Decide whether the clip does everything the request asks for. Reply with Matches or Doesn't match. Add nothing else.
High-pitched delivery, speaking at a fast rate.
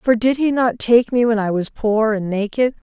Matches